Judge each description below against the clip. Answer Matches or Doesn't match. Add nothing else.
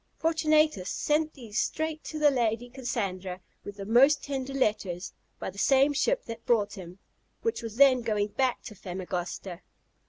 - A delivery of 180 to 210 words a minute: Doesn't match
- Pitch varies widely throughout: Matches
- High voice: Matches